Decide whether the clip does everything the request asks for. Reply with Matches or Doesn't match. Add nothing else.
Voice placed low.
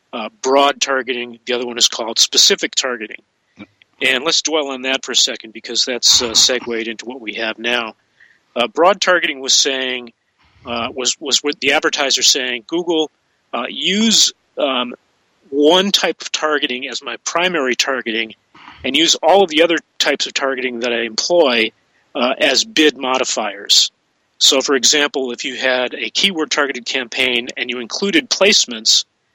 Matches